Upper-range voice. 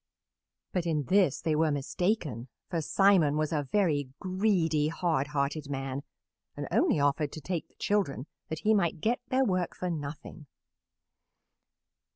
No: medium, 160 Hz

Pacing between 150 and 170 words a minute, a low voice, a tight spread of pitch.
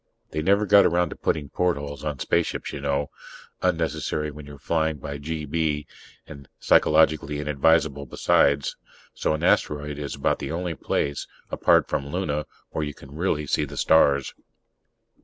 Yes: average, 155 wpm; very low, 75 Hz; narrow, 2.0 semitones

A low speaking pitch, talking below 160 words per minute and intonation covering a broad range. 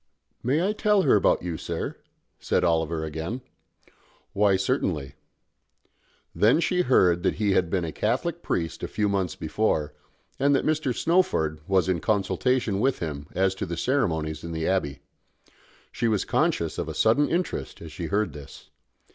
No: very low, 95 Hz; average, 165 wpm; wide, 7.8 semitones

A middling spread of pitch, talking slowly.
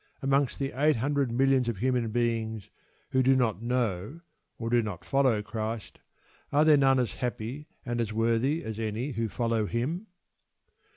No: average, 3.3 semitones; average, 165 wpm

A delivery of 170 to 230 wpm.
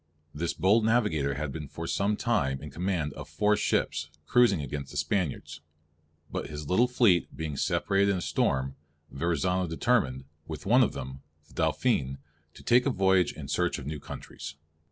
Yes: average, 175 wpm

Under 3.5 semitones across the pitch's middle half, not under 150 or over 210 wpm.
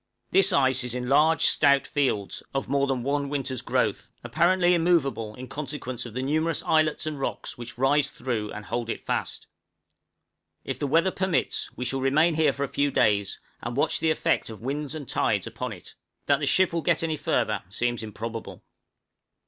No: average, 4.3 semitones; average, 190 wpm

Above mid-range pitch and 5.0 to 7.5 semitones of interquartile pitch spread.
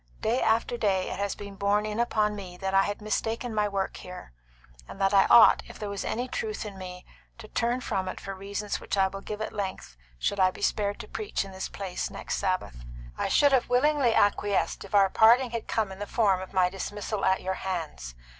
No: high, 200 Hz; narrow, 2.6 semitones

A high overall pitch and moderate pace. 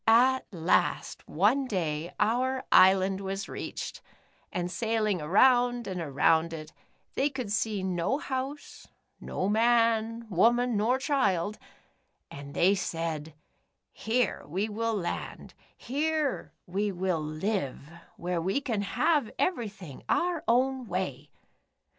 No: high, 210 Hz; slow, 125 wpm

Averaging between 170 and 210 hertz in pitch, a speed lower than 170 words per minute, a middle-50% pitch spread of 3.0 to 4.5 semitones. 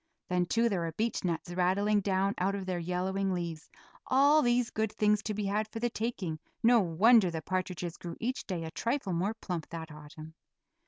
No: high, 190 Hz; average, 195 wpm; average, 4.1 semitones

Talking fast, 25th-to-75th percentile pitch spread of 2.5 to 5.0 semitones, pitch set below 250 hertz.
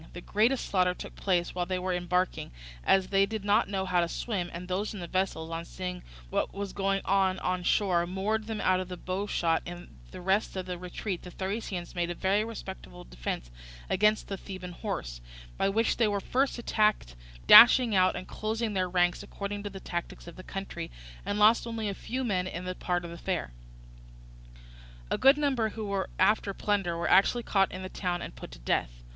Yes: fast, 210 wpm; average, 2.8 semitones; high, 190 Hz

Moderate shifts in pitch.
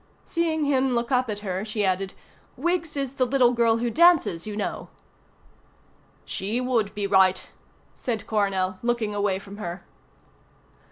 Yes: average, 4.5 semitones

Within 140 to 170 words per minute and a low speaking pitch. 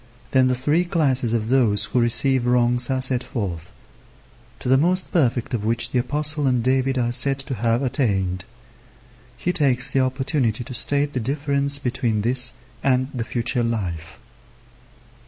Yes: average, 160 wpm; low, 125 Hz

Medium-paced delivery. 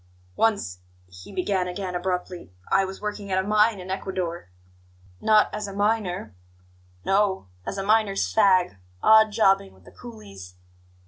Yes: average, 150 wpm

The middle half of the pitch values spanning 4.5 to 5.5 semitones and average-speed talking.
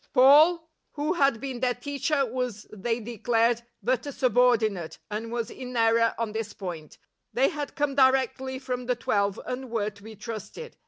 No: average, 2.9 semitones; average, 170 wpm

